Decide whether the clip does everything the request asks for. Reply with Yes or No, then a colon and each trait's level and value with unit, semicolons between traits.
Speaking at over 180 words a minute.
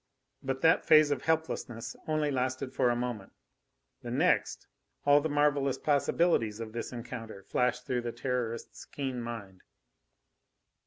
No: average, 140 wpm